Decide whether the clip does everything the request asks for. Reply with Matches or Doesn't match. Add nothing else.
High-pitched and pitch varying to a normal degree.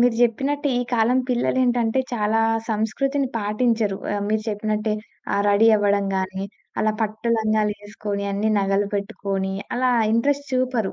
Matches